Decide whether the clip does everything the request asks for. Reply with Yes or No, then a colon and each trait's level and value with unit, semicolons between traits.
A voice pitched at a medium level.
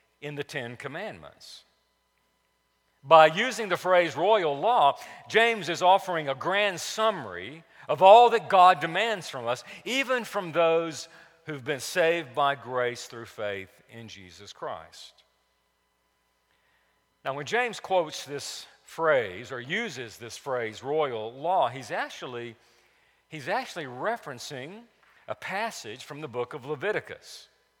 Yes: medium, 155 Hz